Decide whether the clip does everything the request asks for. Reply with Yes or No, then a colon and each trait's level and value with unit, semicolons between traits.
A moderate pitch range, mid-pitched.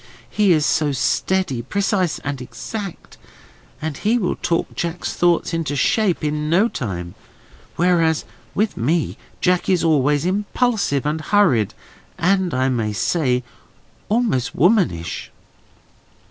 No: wide, 6.1 semitones; medium, 165 Hz